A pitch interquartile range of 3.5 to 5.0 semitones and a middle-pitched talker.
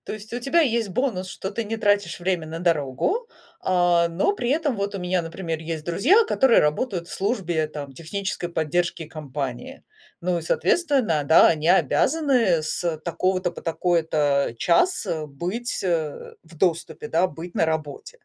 Yes: average, 4.4 semitones; medium, 175 Hz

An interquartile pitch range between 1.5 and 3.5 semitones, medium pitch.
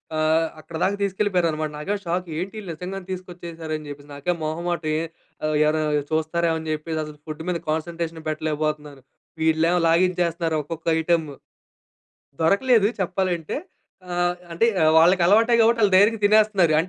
Yes: average, 2.9 semitones; medium, 170 Hz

